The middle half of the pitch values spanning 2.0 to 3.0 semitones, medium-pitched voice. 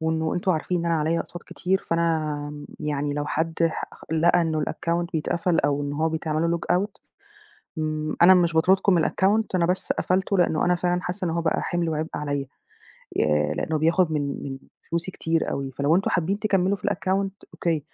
Yes: narrow, 2.5 semitones; medium, 165 Hz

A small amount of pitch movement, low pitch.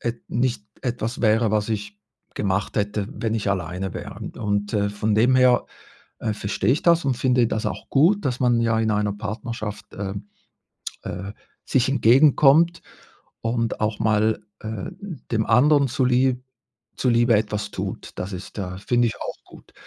No: average, 3.2 semitones; low, 110 Hz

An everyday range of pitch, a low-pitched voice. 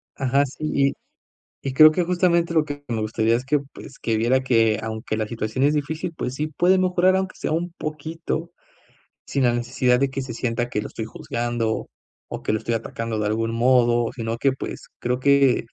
Yes: average, 4.9 semitones; low, 130 Hz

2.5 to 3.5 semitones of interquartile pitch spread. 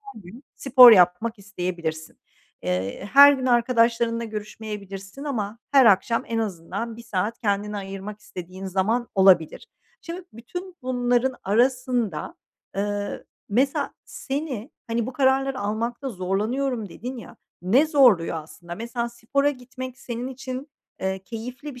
No: average, 4.5 semitones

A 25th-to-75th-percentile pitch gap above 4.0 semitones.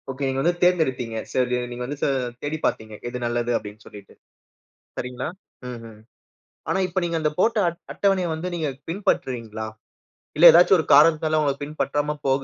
Yes: average, 5.3 semitones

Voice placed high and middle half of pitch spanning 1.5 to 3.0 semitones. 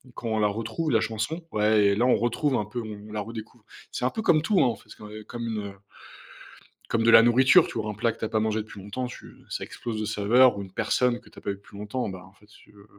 No: low, 110 Hz; narrow, 2.4 semitones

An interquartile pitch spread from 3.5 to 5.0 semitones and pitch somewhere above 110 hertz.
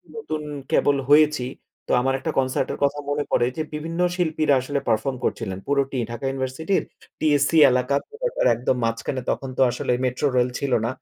No: average, 2.9 semitones; medium, 140 Hz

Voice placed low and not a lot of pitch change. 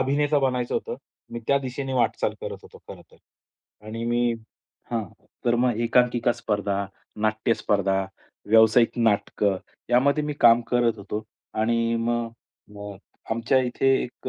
Yes: low, 120 Hz; narrow, 2.2 semitones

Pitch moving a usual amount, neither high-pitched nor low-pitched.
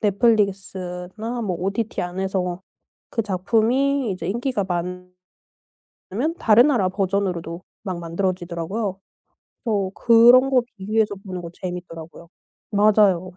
No: average, 3.6 semitones; high, 195 Hz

